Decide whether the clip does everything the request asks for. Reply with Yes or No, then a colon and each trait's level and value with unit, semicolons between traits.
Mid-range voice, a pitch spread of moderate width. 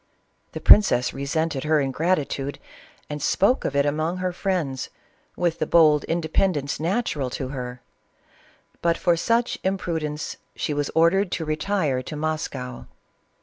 Yes: medium, 155 Hz; average, 3.8 semitones